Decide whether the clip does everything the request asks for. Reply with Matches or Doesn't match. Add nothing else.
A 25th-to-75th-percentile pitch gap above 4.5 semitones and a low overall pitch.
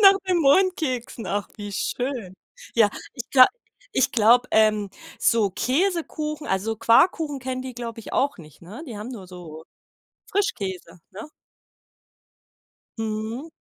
Doesn't match